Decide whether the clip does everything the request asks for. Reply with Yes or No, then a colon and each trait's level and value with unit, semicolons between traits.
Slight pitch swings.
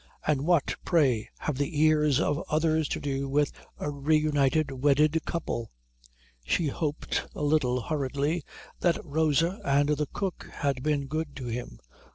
Yes: narrow, 2.2 semitones